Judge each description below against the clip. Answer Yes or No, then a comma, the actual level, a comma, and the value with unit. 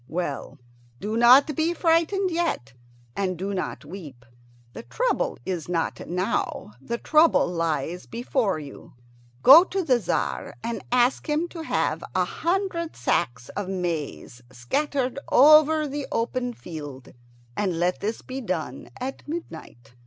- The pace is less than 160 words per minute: Yes, average, 140 wpm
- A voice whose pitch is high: Yes, high, 230 Hz